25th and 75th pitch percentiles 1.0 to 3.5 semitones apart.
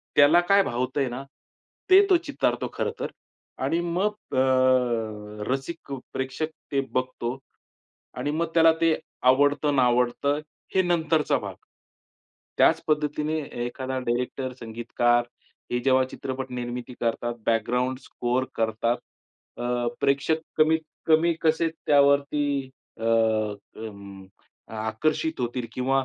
No: average, 3.9 semitones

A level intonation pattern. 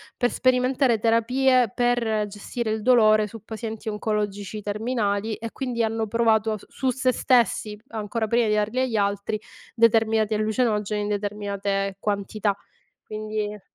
Yes: narrow, 2.0 semitones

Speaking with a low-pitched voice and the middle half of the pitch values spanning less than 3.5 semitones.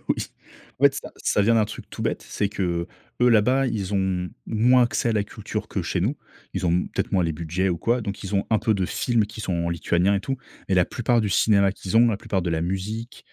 No: low, 100 Hz; average, 3.8 semitones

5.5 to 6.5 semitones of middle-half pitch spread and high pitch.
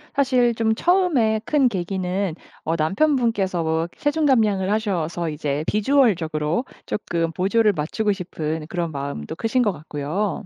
Yes: wide, 6.0 semitones; high, 195 Hz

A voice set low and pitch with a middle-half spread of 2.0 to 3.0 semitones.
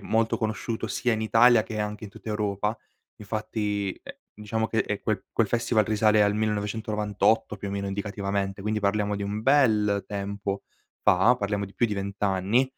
No: low, 105 Hz; narrow, 1.6 semitones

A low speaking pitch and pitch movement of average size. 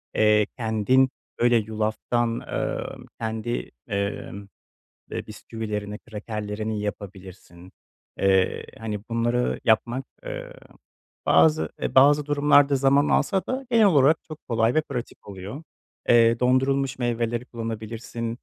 Yes: low, 115 Hz; average, 3.9 semitones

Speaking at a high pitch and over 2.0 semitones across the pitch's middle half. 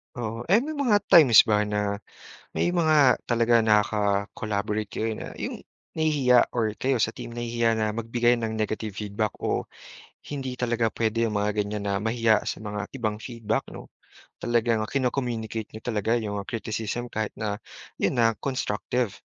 No: low, 115 Hz; narrow, 2.4 semitones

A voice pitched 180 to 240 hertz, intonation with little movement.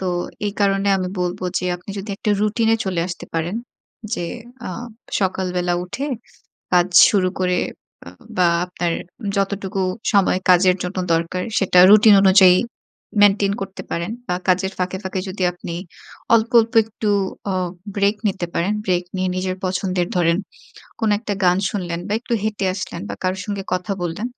Yes: medium, 185 Hz; narrow, 2.0 semitones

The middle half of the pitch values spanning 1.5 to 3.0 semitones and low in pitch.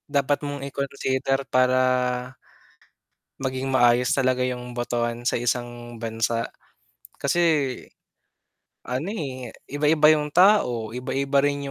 Yes: average, 2.7 semitones; low, 130 Hz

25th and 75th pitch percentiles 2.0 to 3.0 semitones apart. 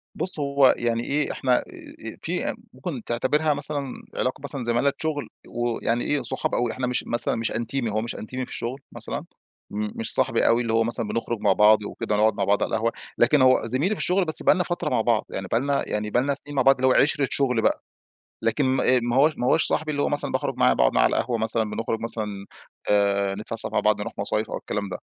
No: average, 3.8 semitones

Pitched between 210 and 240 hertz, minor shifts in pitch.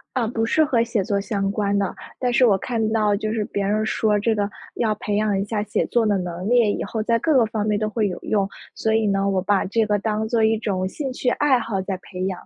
Yes: high, 215 Hz; narrow, 2.2 semitones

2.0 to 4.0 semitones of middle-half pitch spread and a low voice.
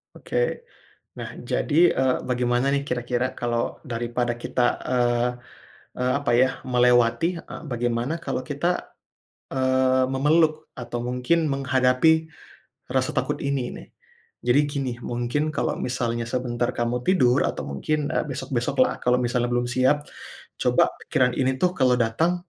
Yes: average, 3.0 semitones; low, 130 Hz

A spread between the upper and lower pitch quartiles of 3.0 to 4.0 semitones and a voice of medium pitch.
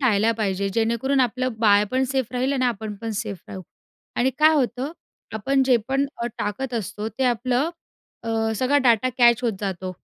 No: average, 3.3 semitones; high, 235 Hz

